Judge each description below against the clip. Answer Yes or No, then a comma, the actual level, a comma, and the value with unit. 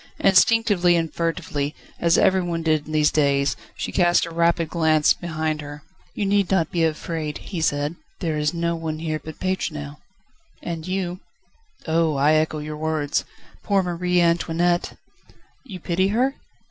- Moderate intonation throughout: No, narrow, 2.3 semitones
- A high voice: No, medium, 165 Hz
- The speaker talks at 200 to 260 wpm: No, average, 155 wpm